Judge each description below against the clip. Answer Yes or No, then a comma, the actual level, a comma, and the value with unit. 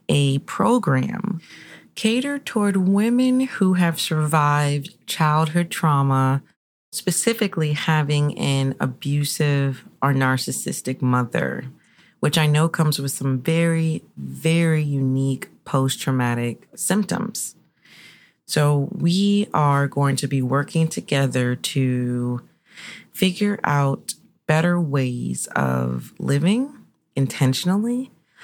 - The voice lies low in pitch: No, medium, 150 Hz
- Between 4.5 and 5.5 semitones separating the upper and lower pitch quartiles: Yes, average, 5.0 semitones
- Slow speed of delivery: Yes, slow, 95 wpm